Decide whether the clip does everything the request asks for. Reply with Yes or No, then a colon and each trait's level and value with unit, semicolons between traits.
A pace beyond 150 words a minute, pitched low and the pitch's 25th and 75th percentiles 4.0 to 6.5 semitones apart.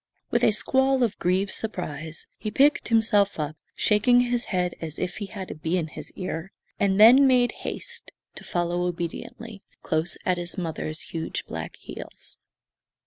No: average, 165 wpm; high, 190 Hz; average, 4.8 semitones